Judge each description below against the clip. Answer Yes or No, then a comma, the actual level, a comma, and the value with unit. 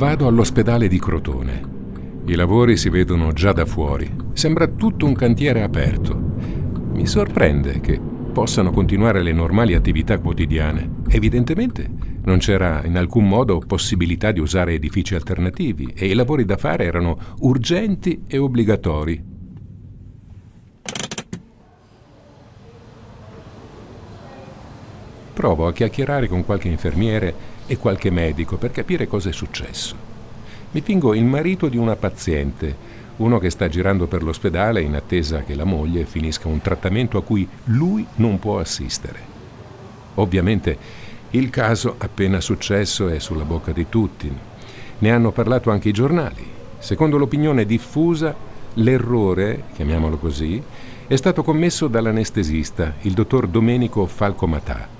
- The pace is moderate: Yes, average, 125 wpm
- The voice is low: Yes, low, 105 Hz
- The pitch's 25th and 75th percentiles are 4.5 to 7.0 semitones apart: Yes, average, 5.2 semitones